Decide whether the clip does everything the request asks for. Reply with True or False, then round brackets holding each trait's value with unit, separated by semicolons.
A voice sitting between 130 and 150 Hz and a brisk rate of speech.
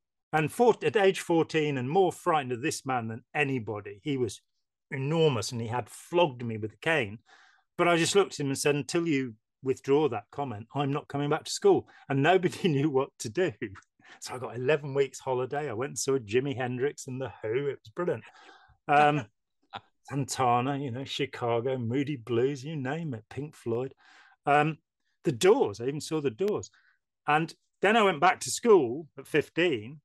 False (140 Hz; 190 wpm)